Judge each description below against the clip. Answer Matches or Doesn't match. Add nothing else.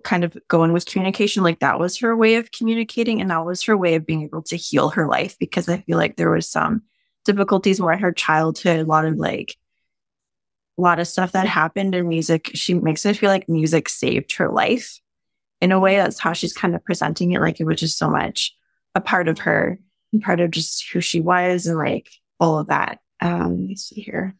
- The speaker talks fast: Matches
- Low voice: Doesn't match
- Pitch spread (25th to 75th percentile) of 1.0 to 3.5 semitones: Matches